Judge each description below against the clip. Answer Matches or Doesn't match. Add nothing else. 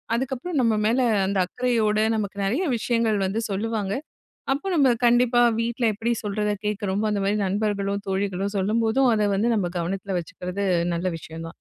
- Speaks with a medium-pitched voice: Doesn't match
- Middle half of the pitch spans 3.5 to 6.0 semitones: Doesn't match